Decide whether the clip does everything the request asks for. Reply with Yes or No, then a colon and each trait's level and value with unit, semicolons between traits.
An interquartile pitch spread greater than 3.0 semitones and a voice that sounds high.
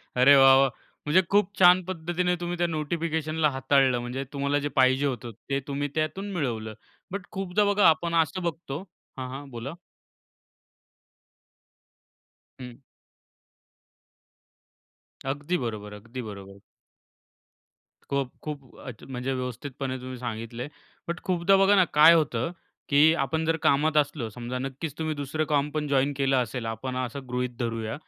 No: average, 4.2 semitones; medium, 140 Hz